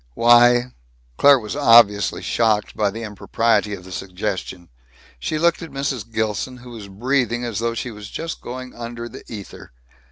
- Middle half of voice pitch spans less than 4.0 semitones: Yes, average, 3.2 semitones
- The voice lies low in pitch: Yes, low, 115 Hz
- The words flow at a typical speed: Yes, average, 170 wpm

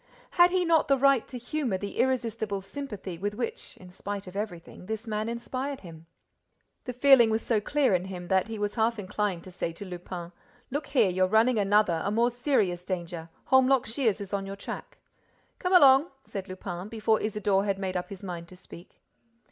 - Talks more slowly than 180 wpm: No, average, 195 wpm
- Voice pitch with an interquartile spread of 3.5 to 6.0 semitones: Yes, average, 4.8 semitones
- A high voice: Yes, high, 210 Hz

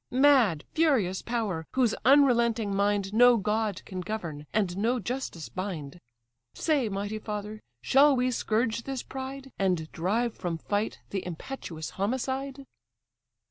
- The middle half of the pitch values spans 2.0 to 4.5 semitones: No, average, 5.1 semitones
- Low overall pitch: No, high, 215 Hz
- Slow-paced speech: Yes, slow, 130 wpm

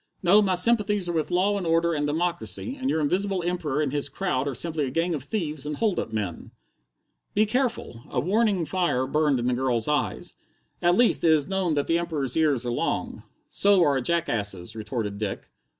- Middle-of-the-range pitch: Yes, medium, 160 Hz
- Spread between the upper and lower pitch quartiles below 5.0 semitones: No, wide, 5.6 semitones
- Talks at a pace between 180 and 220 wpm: Yes, fast, 205 wpm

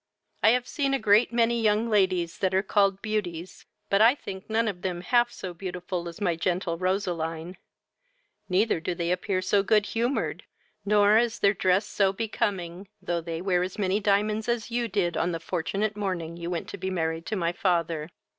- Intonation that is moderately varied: Yes, average, 3.4 semitones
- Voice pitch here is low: No, high, 190 Hz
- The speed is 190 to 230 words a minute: Yes, average, 195 wpm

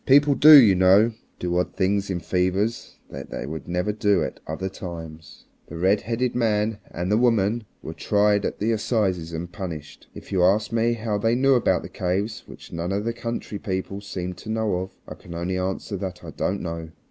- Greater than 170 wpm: Yes, fast, 205 wpm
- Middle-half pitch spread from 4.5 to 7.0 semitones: No, average, 3.7 semitones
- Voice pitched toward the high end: No, low, 100 Hz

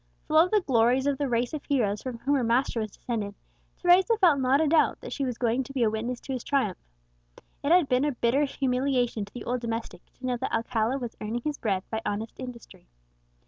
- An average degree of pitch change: Yes, average, 3.4 semitones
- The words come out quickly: Yes, fast, 230 wpm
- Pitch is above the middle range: Yes, very high, 250 Hz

